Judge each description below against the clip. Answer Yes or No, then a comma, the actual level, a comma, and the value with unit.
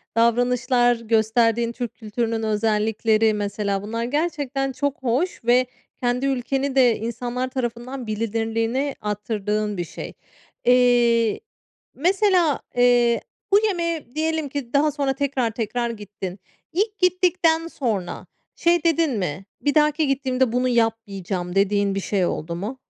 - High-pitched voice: Yes, high, 240 Hz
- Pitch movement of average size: Yes, average, 4.1 semitones